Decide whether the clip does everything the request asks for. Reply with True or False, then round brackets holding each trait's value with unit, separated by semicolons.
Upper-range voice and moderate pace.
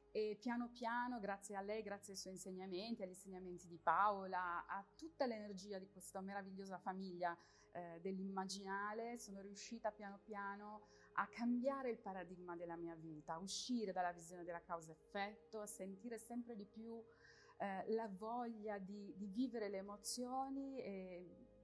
True (200 Hz; 150 wpm)